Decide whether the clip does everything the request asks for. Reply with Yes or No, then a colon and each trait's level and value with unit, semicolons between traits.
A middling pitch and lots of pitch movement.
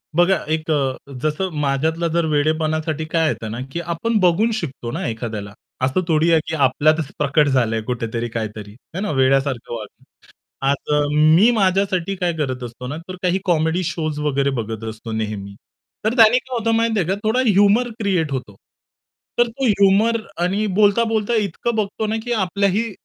Yes: medium, 160 Hz; wide, 6.9 semitones